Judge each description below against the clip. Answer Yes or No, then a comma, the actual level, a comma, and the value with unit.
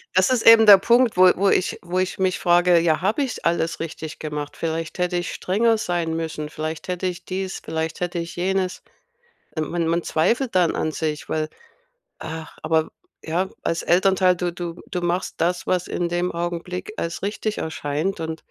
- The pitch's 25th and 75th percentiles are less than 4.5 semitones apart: Yes, narrow, 2.4 semitones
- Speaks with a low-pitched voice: No, medium, 175 Hz